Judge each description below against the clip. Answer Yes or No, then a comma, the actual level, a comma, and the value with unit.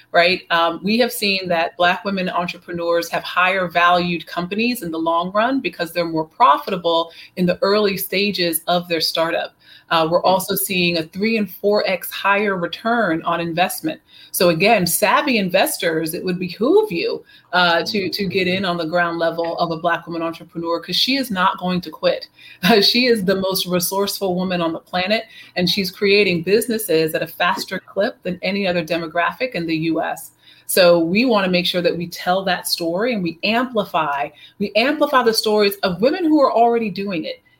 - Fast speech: No, average, 190 wpm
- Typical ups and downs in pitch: Yes, average, 3.4 semitones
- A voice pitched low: No, medium, 180 Hz